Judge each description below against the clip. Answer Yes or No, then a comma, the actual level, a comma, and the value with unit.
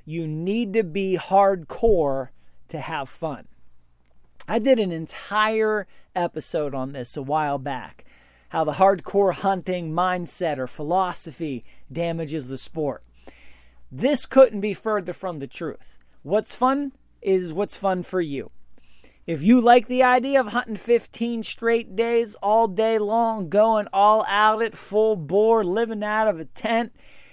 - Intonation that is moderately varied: No, wide, 6.1 semitones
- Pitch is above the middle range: Yes, high, 195 Hz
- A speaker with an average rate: Yes, average, 145 wpm